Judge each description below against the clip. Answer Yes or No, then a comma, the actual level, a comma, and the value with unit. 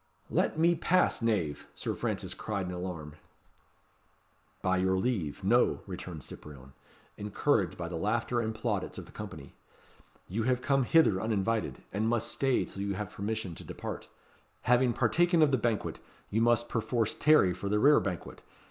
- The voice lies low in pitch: Yes, low, 105 Hz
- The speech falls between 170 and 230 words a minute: No, average, 160 wpm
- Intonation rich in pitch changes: No, average, 4.3 semitones